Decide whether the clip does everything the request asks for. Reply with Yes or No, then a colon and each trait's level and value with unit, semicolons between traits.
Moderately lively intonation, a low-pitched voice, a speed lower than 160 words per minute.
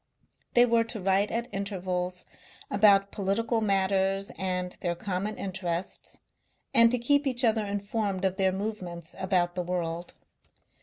No: average, 3.0 semitones; high, 195 Hz; average, 140 wpm